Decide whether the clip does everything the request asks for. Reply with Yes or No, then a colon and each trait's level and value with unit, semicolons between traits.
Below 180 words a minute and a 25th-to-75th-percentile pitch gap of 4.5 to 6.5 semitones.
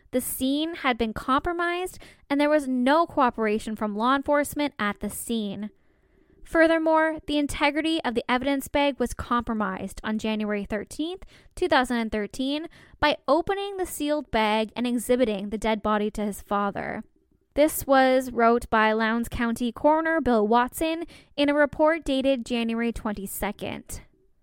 Yes: average, 140 wpm; average, 5.2 semitones